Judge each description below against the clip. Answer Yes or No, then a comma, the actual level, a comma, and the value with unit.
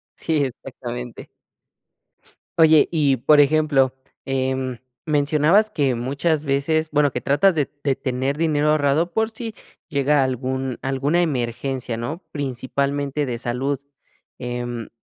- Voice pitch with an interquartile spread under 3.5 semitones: Yes, average, 2.8 semitones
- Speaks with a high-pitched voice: No, medium, 140 Hz